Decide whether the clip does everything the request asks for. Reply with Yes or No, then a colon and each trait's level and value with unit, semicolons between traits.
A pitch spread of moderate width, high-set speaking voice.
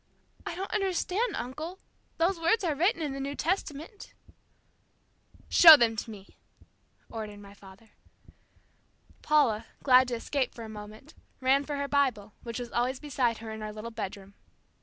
No: wide, 5.9 semitones; very high, 260 Hz